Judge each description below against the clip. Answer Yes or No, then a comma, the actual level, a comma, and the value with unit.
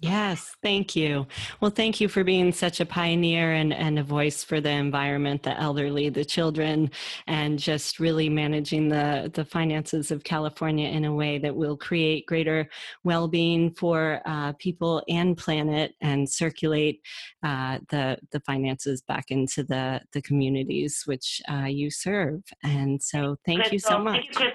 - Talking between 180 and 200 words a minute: No, average, 160 wpm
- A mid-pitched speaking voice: Yes, medium, 155 Hz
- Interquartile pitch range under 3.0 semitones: Yes, narrow, 2.6 semitones